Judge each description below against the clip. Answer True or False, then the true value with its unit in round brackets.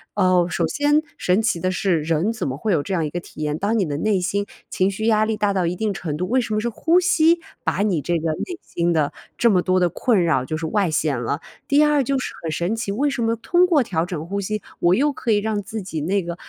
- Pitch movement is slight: False (5.0 semitones)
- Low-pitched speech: False (195 Hz)